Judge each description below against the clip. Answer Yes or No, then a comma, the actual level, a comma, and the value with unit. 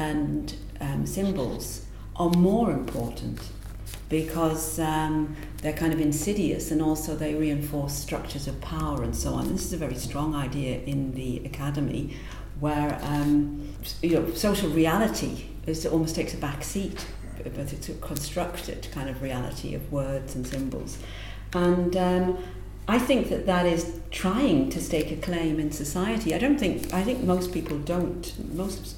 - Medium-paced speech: Yes, average, 160 wpm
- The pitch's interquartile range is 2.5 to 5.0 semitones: Yes, average, 4.2 semitones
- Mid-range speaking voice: Yes, medium, 150 Hz